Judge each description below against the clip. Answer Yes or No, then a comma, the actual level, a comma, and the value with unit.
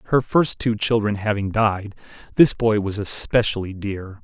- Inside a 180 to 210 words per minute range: No, average, 155 wpm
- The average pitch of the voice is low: Yes, low, 105 Hz